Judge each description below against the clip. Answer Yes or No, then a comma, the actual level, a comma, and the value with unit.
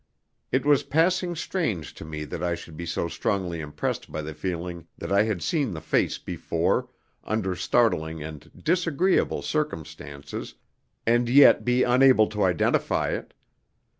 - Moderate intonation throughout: No, wide, 9.0 semitones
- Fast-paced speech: No, average, 150 wpm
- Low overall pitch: Yes, very low, 95 Hz